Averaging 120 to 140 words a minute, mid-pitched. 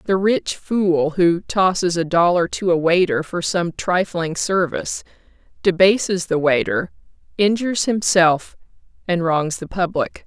Yes: slow, 135 wpm; medium, 180 Hz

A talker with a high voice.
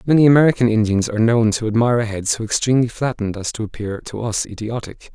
No: low, 115 Hz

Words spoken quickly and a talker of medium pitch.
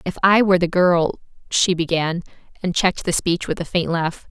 Yes: fast, 210 wpm; medium, 175 Hz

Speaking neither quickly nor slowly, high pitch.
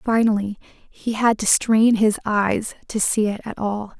Yes: average, 180 wpm; high, 215 Hz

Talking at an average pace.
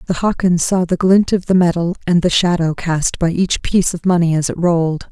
No: fast, 235 wpm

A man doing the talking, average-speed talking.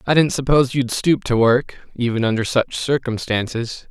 Yes: male; average, 170 wpm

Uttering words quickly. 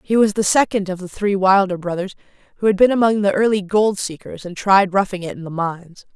Yes: fast, 235 wpm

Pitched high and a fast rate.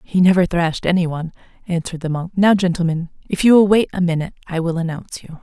No: medium, 175 Hz; fast, 220 wpm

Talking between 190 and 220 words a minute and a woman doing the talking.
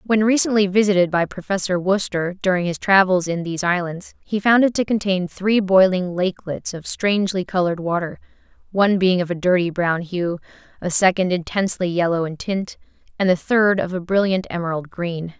No: average, 175 wpm; female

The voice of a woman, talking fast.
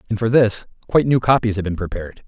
No: male; fast, 235 wpm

